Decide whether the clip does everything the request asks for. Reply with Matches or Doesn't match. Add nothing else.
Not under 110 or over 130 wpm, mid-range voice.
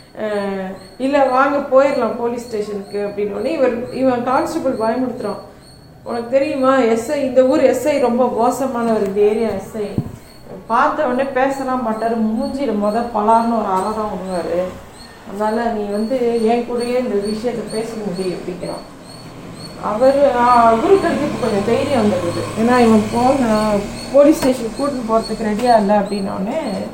Doesn't match